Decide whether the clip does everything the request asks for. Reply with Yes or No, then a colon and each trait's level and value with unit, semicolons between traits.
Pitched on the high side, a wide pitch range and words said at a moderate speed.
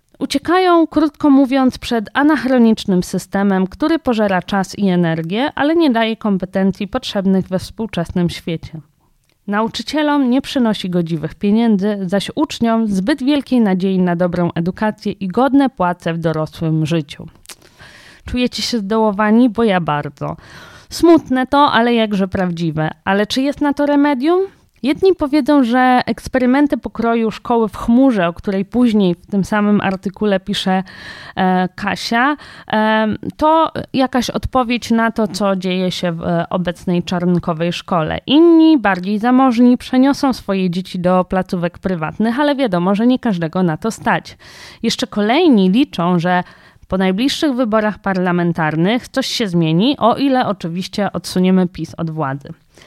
Yes: high, 210 Hz; wide, 5.9 semitones; average, 135 wpm